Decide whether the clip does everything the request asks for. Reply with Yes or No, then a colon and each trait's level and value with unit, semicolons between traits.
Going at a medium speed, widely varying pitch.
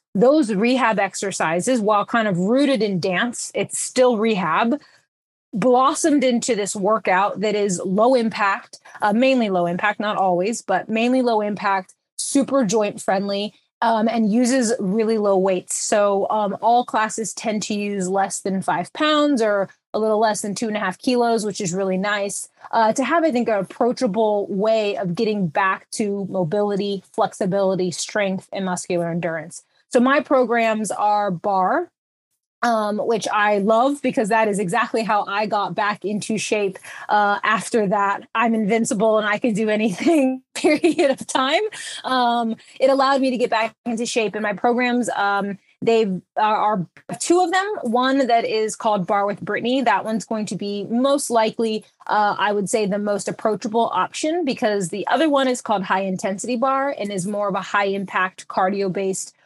No: average, 175 wpm; average, 3.2 semitones